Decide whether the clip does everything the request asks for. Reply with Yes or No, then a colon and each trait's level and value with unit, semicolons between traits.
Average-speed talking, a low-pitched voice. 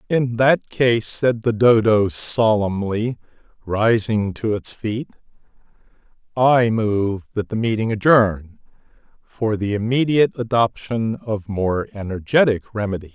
No: slow, 115 wpm; low, 110 Hz